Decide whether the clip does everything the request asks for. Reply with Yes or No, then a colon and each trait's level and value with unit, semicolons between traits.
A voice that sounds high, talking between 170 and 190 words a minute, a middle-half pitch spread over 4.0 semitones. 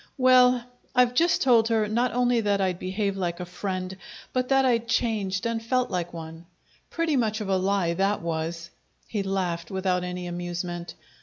Yes: high, 195 Hz; average, 175 wpm; average, 4.9 semitones